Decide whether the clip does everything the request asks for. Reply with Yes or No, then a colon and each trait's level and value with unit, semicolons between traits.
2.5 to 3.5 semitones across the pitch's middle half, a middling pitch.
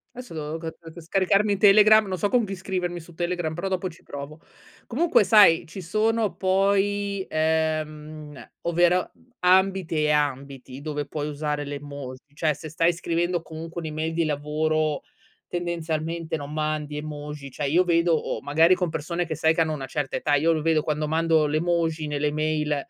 Yes: average, 2.8 semitones; medium, 160 Hz